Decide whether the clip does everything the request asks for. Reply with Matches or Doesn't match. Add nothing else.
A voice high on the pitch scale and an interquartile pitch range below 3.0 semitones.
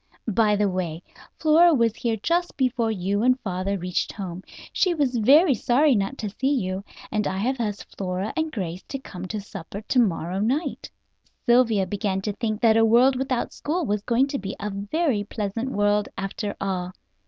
Doesn't match